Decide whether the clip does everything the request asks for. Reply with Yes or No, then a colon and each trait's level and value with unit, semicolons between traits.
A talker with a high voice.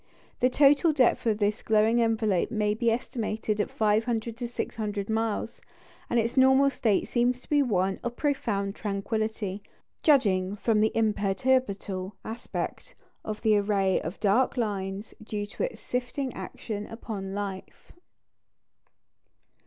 Yes: high, 220 Hz